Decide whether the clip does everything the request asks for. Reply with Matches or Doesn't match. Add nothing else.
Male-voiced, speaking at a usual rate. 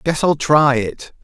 Matches